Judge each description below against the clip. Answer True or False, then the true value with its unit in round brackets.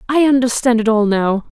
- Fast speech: False (190 wpm)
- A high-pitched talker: True (235 Hz)